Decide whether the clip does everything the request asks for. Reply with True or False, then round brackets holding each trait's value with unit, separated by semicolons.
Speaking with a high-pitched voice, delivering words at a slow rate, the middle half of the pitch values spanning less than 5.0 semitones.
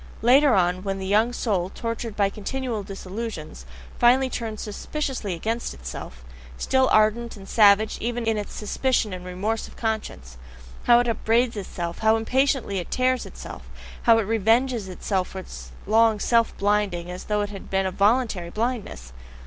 False (215 Hz; 165 wpm; 3.6 semitones)